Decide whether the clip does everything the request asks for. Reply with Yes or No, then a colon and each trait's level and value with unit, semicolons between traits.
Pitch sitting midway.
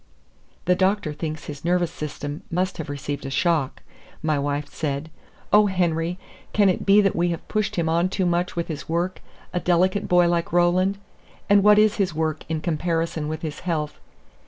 Yes: medium, 170 Hz